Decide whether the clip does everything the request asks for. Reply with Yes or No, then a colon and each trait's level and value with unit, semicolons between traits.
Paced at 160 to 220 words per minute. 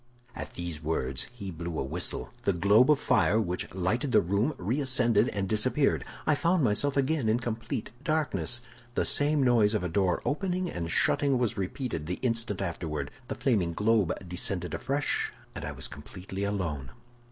Yes: average, 170 wpm